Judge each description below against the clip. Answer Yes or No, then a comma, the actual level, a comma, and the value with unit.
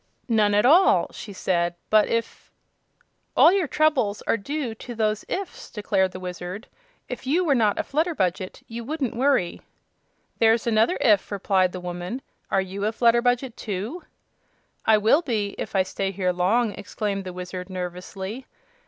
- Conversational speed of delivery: Yes, average, 160 wpm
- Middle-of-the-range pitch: No, high, 215 Hz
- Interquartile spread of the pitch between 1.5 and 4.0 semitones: No, average, 4.8 semitones